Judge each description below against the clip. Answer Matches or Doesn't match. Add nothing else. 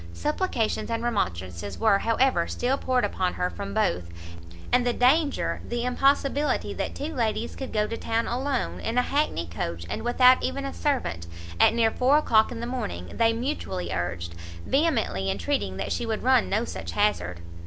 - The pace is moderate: Matches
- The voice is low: Doesn't match